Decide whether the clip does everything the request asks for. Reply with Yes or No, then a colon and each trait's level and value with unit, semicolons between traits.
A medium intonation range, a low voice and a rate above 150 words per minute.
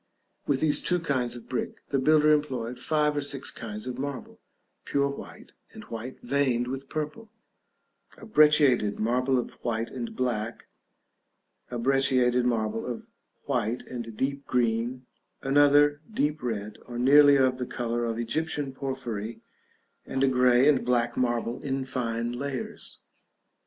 No: average, 3.0 semitones; low, 130 Hz; average, 145 wpm